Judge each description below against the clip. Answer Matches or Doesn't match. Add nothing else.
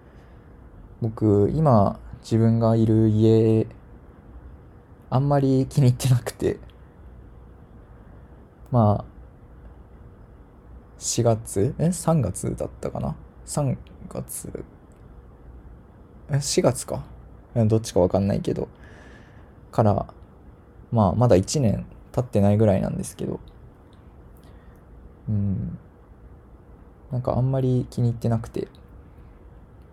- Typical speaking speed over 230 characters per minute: Doesn't match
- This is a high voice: Doesn't match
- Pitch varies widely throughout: Doesn't match